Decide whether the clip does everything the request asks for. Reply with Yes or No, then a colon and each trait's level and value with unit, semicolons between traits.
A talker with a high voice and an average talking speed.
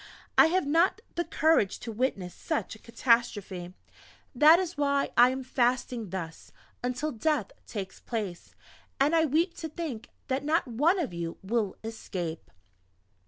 Yes: very high, 250 Hz; average, 150 wpm